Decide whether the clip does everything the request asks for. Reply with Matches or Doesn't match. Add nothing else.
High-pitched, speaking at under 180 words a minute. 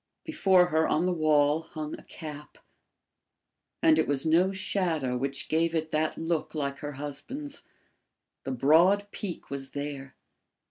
Doesn't match